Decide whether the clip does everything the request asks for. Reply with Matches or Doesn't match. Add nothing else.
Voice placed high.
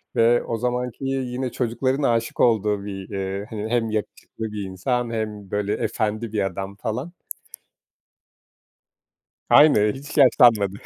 Doesn't match